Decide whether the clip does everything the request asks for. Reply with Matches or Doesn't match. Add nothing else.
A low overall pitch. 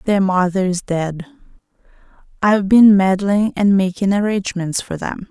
Doesn't match